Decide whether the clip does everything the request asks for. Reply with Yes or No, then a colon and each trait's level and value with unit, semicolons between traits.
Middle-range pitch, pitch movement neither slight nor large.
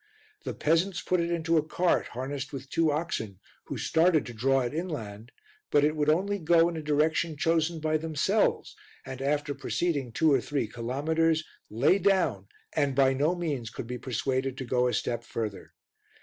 Yes: medium, 150 Hz; average, 4.1 semitones